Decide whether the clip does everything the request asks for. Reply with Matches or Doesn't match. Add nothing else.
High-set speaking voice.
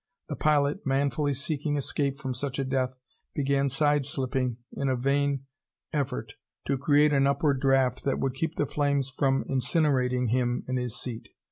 Doesn't match